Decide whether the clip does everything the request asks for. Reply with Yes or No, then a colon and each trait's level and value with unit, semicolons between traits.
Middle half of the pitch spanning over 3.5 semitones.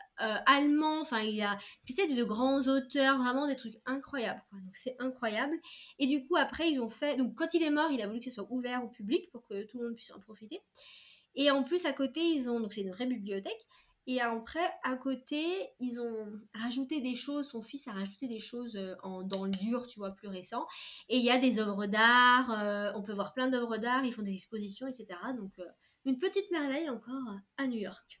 Yes: average, 4.3 semitones